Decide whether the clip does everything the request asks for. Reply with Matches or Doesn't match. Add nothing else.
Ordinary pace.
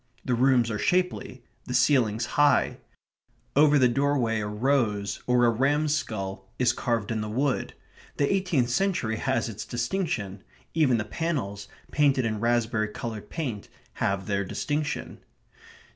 Matches